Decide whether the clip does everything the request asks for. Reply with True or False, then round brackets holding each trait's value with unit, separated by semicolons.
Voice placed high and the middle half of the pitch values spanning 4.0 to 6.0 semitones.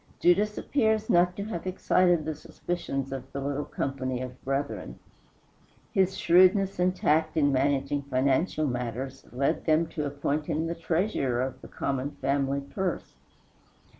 False (145 Hz; 4.6 semitones)